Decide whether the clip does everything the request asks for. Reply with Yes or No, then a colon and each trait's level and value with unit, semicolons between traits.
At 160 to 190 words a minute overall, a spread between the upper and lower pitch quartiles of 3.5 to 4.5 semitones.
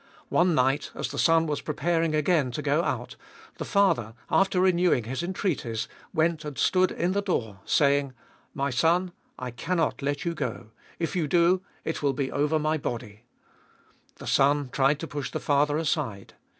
Yes: average, 180 wpm; average, 3.9 semitones